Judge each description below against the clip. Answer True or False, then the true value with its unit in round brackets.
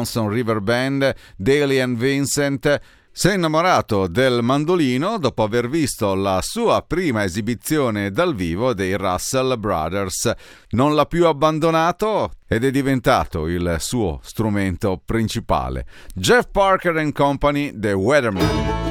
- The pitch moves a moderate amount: False (6.2 semitones)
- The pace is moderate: True (125 wpm)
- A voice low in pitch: True (120 Hz)